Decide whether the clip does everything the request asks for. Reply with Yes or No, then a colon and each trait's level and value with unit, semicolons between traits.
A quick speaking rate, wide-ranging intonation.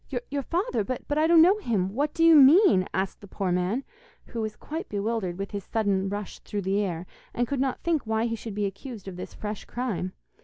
Yes: fast, 225 wpm; wide, 6.1 semitones